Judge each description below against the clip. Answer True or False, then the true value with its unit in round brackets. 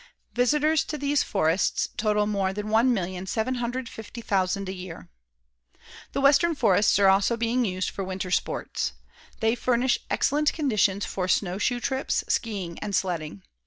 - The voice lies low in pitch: False (210 Hz)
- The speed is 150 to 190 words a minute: False (135 wpm)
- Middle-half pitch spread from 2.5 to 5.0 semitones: True (4.6 semitones)